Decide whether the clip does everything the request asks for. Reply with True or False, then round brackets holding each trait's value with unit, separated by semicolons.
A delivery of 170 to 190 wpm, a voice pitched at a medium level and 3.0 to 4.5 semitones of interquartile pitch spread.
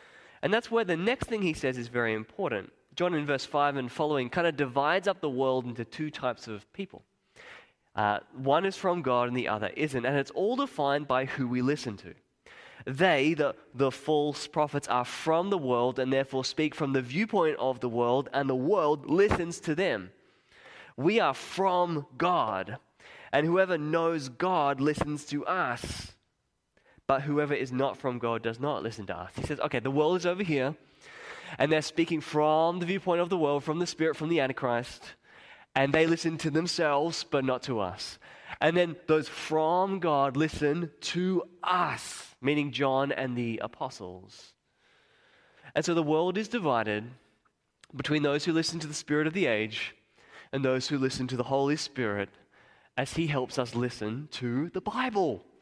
True (180 wpm; 145 Hz; 4.2 semitones)